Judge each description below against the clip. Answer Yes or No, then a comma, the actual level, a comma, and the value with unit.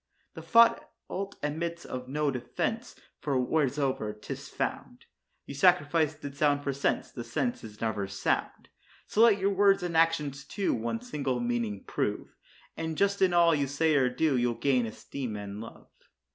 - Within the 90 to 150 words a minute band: No, average, 165 wpm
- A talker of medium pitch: Yes, medium, 145 Hz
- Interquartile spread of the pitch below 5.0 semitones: No, wide, 5.5 semitones